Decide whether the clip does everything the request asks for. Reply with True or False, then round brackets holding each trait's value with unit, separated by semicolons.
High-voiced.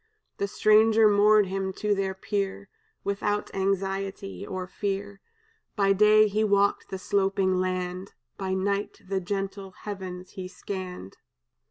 True (195 Hz)